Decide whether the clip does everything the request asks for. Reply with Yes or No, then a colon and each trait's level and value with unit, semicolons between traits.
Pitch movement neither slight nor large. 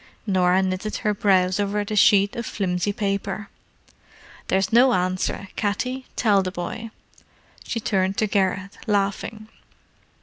No: narrow, 2.1 semitones